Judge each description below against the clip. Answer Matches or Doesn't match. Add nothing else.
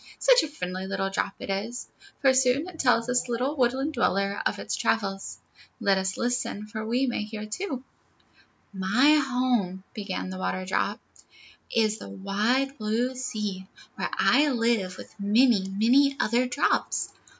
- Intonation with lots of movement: Doesn't match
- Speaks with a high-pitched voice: Matches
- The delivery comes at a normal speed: Matches